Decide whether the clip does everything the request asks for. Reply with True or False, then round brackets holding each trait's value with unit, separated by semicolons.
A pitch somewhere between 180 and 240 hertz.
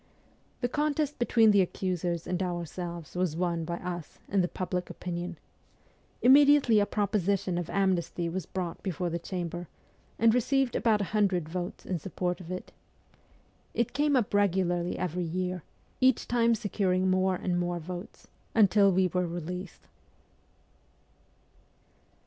True (185 Hz)